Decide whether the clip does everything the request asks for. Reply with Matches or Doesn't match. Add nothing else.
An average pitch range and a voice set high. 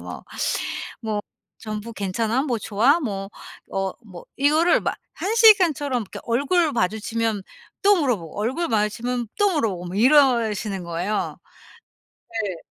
Doesn't match